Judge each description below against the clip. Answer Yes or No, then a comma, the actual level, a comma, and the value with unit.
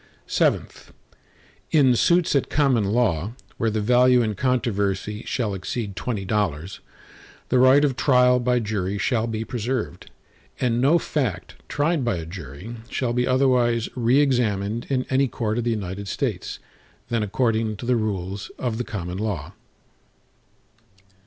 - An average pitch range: Yes, average, 3.7 semitones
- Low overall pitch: Yes, low, 115 Hz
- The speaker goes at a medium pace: Yes, average, 145 wpm